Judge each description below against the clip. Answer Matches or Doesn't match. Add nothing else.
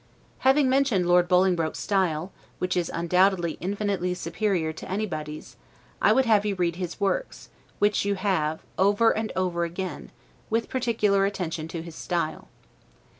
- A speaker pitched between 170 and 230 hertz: Matches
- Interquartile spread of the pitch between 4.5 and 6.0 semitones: Doesn't match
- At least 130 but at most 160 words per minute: Matches